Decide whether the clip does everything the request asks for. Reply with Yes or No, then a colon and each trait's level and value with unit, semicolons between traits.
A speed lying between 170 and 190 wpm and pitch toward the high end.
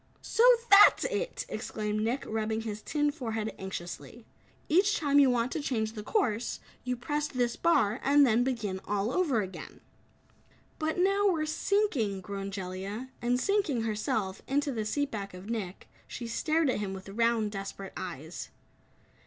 No: average, 160 wpm; high, 230 Hz